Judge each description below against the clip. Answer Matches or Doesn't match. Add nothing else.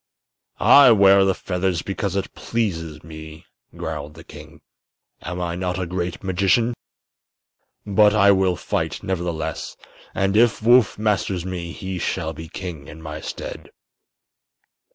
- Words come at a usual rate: Doesn't match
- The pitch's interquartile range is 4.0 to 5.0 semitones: Doesn't match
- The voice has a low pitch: Matches